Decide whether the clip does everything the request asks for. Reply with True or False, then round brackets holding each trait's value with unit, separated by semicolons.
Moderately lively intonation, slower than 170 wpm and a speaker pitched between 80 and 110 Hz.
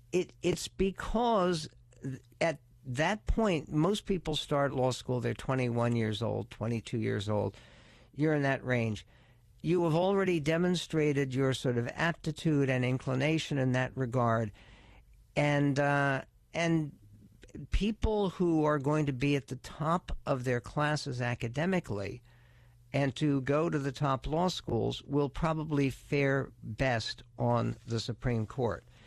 False (4.6 semitones; 140 wpm; 135 Hz)